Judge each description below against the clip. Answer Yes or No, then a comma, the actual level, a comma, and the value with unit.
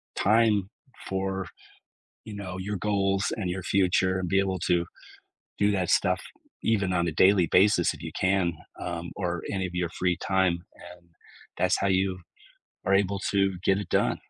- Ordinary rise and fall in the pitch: No, narrow, 1.6 semitones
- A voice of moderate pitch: No, very low, 95 Hz